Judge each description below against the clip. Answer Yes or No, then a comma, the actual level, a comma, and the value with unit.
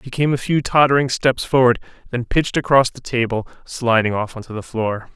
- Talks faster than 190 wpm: Yes, average, 200 wpm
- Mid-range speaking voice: No, low, 125 Hz